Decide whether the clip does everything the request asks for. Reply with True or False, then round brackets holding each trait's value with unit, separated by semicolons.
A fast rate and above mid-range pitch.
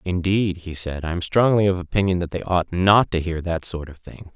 False (250 wpm; 90 Hz)